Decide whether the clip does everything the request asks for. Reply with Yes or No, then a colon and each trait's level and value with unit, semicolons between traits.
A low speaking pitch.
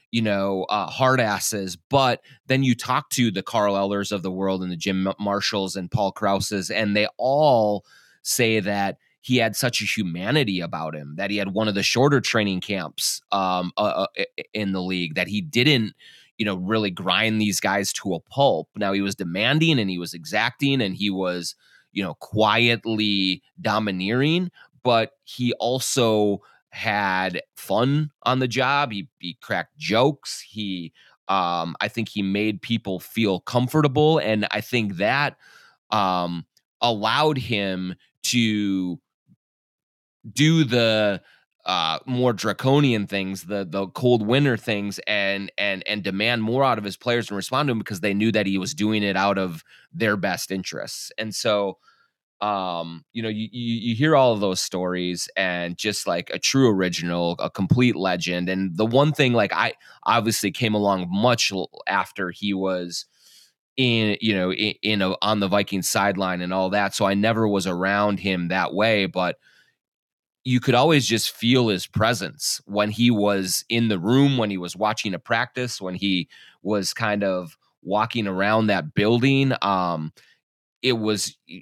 Yes: low, 105 Hz